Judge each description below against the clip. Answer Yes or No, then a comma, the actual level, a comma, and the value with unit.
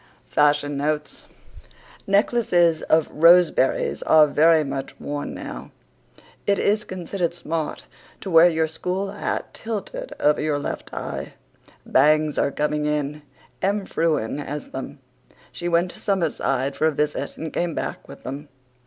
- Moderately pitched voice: Yes, medium, 155 Hz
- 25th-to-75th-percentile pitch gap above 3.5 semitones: No, average, 3.0 semitones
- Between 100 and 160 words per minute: Yes, average, 140 wpm